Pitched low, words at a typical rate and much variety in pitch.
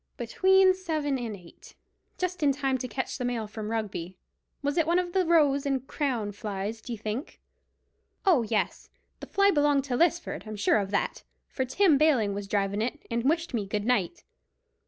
No: very high, 255 Hz; average, 185 wpm; wide, 6.5 semitones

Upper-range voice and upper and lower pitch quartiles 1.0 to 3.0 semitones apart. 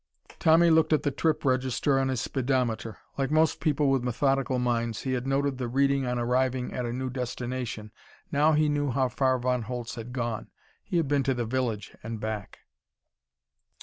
No: low, 130 Hz; narrow, 2.4 semitones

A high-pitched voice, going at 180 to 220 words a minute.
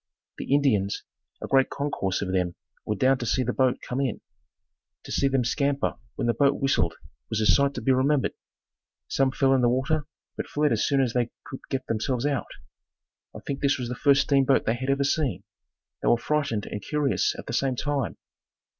No: low, 130 Hz; fast, 205 wpm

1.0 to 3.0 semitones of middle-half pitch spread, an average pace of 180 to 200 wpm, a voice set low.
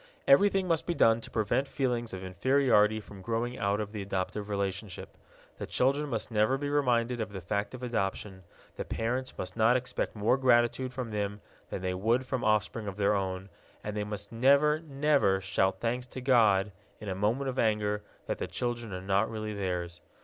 No: average, 4.2 semitones; average, 195 wpm; low, 110 Hz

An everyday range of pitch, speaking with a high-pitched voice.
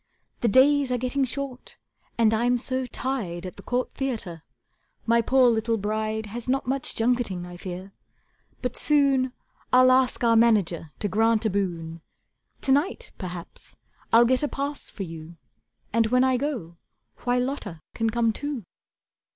Yes: average, 4.3 semitones; high, 235 Hz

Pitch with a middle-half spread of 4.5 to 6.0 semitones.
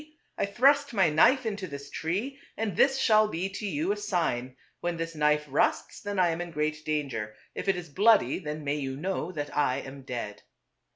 Yes: wide, 5.5 semitones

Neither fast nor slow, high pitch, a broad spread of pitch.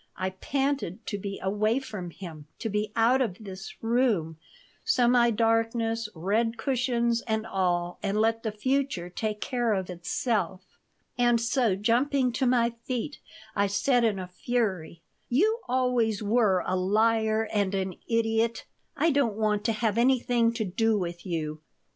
No: average, 155 wpm; high, 225 Hz; average, 3.7 semitones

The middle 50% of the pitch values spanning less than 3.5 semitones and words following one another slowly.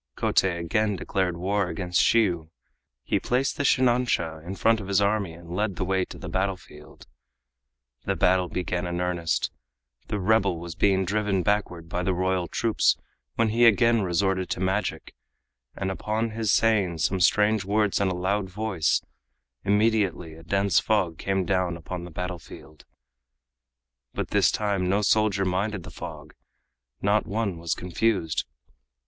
No: average, 3.0 semitones; average, 155 wpm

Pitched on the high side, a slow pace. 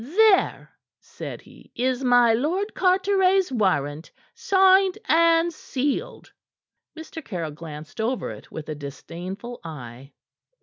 Yes: very high, 255 Hz; slow, 115 wpm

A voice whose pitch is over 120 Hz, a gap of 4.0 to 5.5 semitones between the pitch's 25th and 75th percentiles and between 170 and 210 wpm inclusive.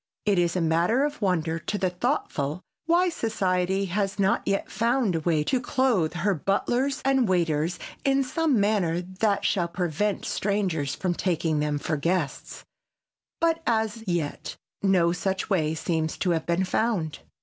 No: medium, 185 Hz; average, 4.8 semitones; average, 160 wpm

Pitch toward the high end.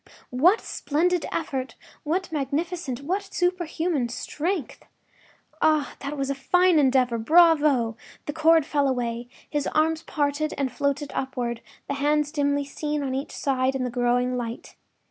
Yes: very high, 285 Hz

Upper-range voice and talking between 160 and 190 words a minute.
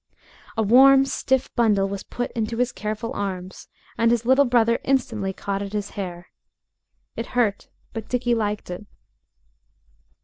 No: high, 225 Hz; average, 145 wpm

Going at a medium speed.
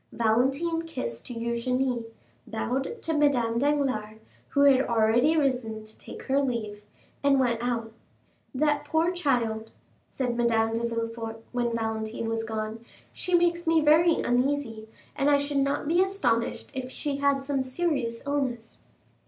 Yes: average, 145 wpm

